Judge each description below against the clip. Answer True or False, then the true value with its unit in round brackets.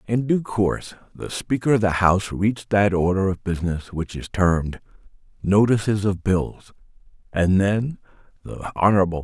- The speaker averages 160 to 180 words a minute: False (150 wpm)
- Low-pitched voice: True (100 Hz)